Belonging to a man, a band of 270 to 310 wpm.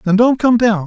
Yes: male; fast, 275 wpm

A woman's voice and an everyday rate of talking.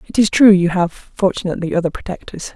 Yes: female; average, 190 wpm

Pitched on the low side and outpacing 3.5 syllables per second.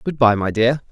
Yes: low, 120 Hz; 5.3 syllables/s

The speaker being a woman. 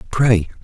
No: male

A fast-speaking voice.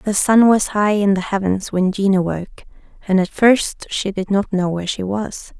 Yes: fast, 215 wpm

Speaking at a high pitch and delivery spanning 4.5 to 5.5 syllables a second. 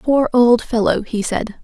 No: high, 235 Hz; 4.0 syllables/s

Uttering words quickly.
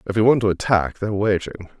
Yes: fast, 235 wpm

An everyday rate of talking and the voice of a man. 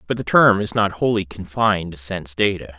No: fast, 215 wpm; male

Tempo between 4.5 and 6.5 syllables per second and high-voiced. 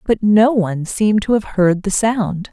Yes: 4.6 syllables/s; high, 200 Hz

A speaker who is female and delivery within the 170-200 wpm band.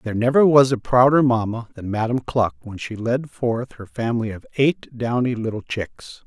No: male; average, 190 wpm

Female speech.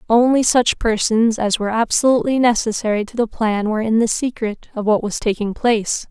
Yes: female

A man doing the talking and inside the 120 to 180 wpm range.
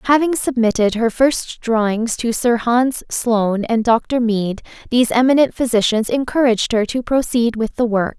No: female; average, 160 wpm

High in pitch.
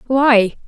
Yes: high, 240 Hz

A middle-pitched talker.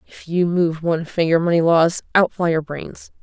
Yes: medium, 170 Hz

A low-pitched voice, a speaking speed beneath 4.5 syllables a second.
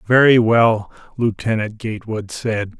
Yes: low, 110 Hz; 4.2 syllables/s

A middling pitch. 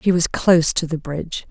Yes: medium, 165 Hz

